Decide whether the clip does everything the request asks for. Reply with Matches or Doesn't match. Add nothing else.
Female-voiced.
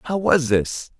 Doesn't match